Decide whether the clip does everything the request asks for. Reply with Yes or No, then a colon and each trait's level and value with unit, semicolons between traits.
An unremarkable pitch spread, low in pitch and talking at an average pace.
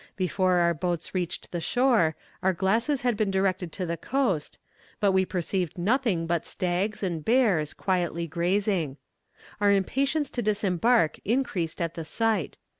No: average, 4.1 semitones; high, 190 Hz; average, 150 wpm